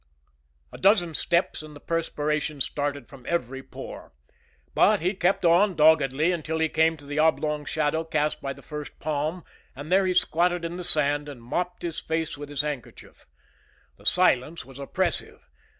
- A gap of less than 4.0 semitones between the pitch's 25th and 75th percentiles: Yes, average, 2.8 semitones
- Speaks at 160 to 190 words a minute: Yes, average, 170 wpm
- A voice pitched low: No, medium, 155 Hz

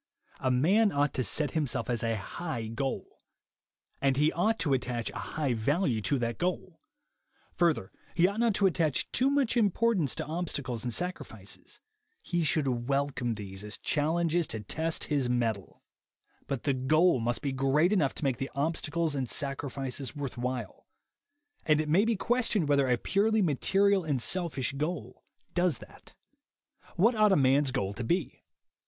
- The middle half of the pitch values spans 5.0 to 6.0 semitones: Yes, wide, 5.6 semitones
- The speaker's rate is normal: Yes, average, 165 wpm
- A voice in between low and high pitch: Yes, medium, 145 Hz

